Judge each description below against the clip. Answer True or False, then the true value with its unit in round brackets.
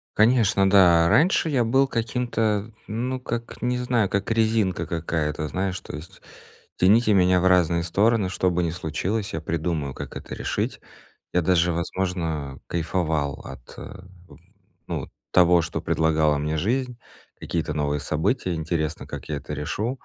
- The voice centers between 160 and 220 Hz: False (90 Hz)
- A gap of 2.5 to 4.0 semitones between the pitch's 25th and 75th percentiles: False (5.5 semitones)